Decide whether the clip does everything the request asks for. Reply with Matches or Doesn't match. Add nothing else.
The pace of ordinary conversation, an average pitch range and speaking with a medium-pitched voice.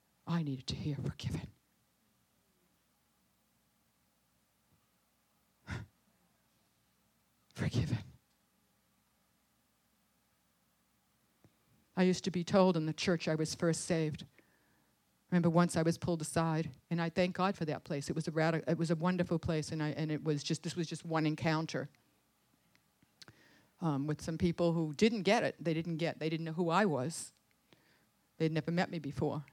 Doesn't match